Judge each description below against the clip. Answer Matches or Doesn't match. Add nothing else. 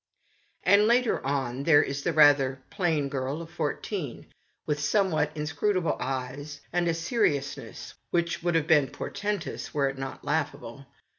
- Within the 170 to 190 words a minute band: Doesn't match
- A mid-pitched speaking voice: Matches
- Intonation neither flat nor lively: Matches